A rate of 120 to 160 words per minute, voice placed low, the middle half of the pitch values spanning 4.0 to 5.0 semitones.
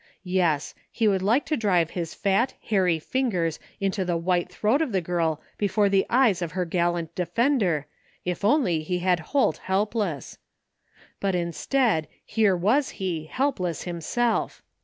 No: average, 155 wpm; medium, 185 Hz; average, 4.3 semitones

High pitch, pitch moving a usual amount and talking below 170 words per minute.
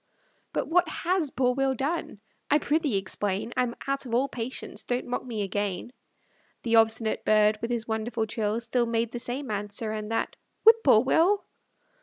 No: high, 235 Hz; average, 3.9 semitones; average, 175 wpm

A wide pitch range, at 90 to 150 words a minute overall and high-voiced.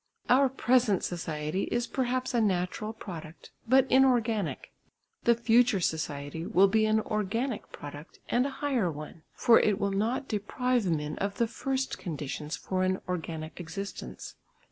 Yes: wide, 6.2 semitones; average, 145 wpm; high, 205 Hz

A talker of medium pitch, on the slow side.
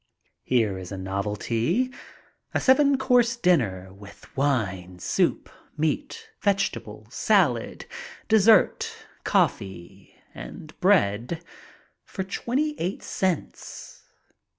Yes: medium, 145 Hz; slow, 90 wpm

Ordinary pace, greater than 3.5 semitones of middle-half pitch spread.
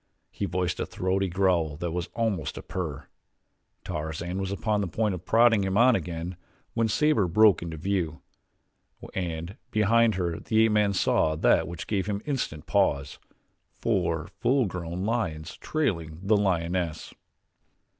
Yes: average, 150 wpm; average, 4.2 semitones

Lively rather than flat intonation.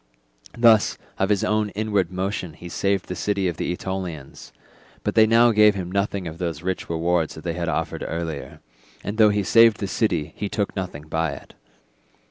No: average, 3.6 semitones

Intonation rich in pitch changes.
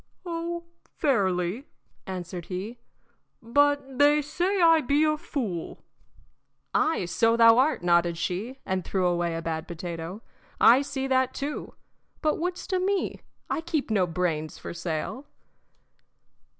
Yes: wide, 8.9 semitones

